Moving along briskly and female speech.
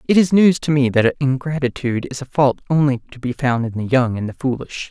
No: fast, 245 wpm; male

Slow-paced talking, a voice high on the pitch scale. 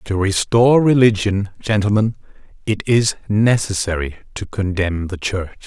No: slow, 115 wpm; low, 105 Hz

